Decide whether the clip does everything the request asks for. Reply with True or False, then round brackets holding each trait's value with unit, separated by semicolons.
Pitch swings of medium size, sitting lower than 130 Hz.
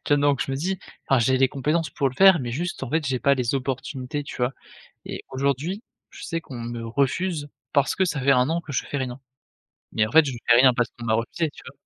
False (3.4 semitones; 135 Hz)